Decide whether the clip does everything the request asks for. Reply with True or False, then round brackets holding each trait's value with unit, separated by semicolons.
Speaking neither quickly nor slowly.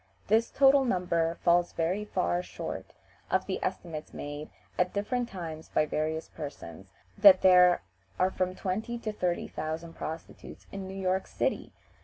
True (150 wpm)